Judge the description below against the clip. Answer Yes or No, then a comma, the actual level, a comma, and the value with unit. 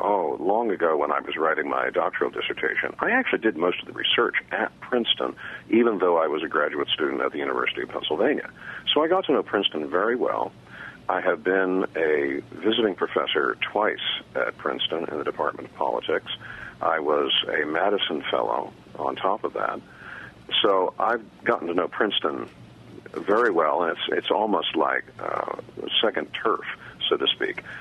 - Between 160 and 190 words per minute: Yes, average, 175 wpm